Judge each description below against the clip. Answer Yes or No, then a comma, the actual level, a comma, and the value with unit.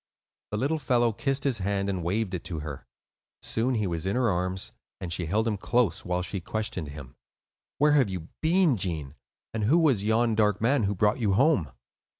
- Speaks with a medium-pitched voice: No, low, 105 Hz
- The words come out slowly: No, average, 200 wpm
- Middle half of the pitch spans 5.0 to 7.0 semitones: Yes, average, 5.3 semitones